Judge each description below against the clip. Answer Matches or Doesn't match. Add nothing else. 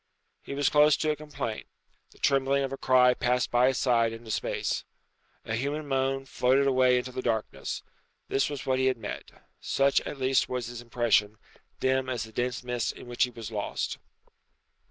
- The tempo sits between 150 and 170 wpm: Doesn't match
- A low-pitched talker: Matches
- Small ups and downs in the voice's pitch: Matches